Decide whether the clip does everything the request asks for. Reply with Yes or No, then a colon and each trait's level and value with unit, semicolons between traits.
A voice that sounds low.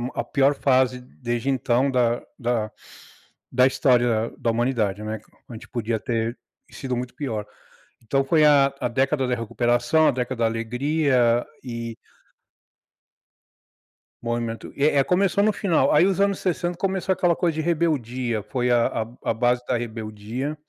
Yes: low, 125 Hz